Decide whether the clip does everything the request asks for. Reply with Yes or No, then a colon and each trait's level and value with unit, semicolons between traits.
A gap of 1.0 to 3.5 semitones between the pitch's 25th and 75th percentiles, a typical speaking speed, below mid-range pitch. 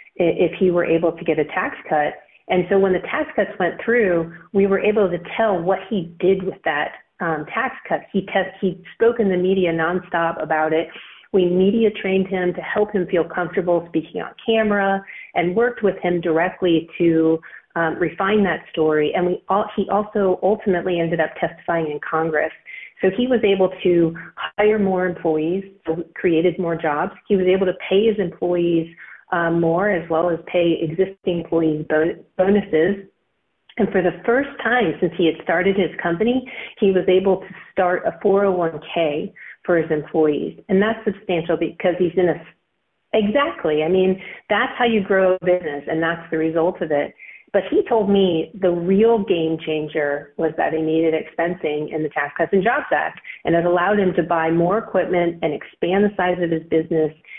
No: average, 3.0 semitones; average, 185 wpm; medium, 180 Hz